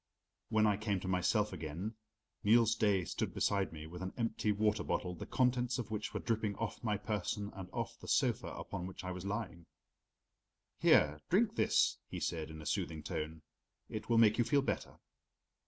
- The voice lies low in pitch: Yes, low, 105 Hz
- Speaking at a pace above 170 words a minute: Yes, average, 190 wpm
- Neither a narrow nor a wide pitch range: Yes, average, 3.9 semitones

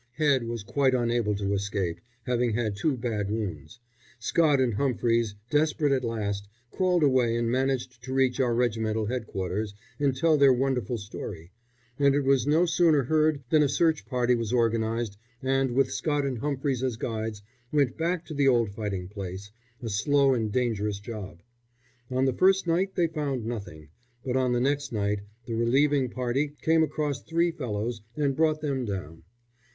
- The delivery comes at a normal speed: Yes, average, 170 wpm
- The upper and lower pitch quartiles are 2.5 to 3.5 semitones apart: No, average, 4.5 semitones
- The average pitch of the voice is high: No, low, 125 Hz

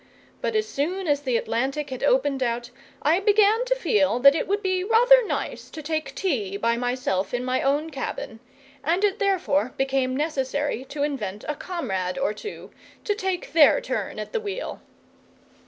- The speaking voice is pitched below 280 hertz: No, very high, 290 Hz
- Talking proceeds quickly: No, average, 175 wpm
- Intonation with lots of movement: Yes, wide, 7.0 semitones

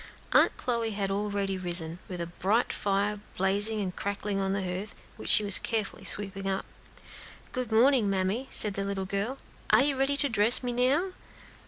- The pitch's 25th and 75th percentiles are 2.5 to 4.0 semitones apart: Yes, average, 3.1 semitones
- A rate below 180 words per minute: No, average, 185 wpm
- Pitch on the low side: No, high, 205 Hz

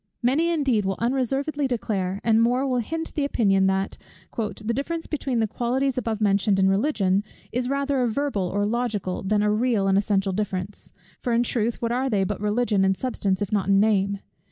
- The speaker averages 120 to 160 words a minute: No, average, 195 wpm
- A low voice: No, high, 220 Hz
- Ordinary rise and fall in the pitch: Yes, average, 4.4 semitones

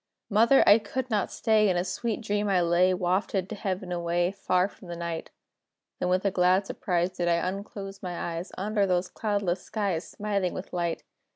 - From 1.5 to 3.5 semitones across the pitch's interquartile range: Yes, narrow, 2.5 semitones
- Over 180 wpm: Yes, average, 190 wpm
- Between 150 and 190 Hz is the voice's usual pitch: Yes, medium, 185 Hz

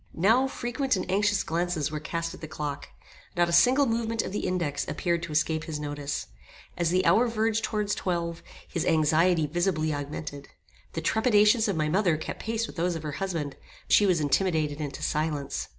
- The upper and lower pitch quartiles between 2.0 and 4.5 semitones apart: No, average, 5.2 semitones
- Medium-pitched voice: Yes, medium, 170 Hz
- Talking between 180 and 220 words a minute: Yes, average, 190 wpm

